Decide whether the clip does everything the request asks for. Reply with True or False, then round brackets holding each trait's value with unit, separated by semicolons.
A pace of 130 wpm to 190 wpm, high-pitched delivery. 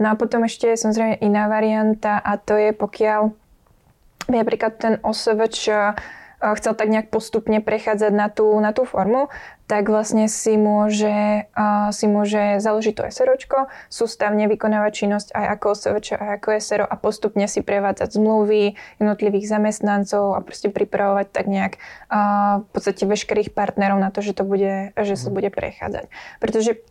True (160 wpm; 210 Hz)